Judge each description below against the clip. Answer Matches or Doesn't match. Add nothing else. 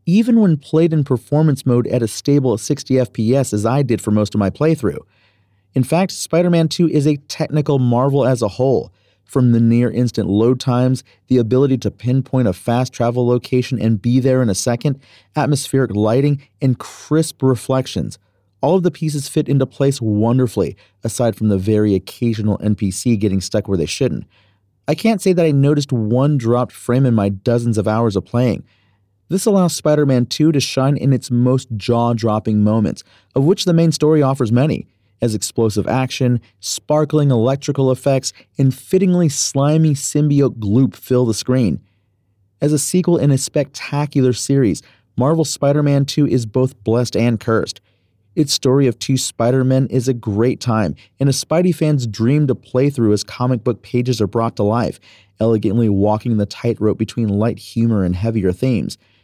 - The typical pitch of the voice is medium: Doesn't match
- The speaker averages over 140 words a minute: Matches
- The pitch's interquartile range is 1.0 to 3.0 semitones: Doesn't match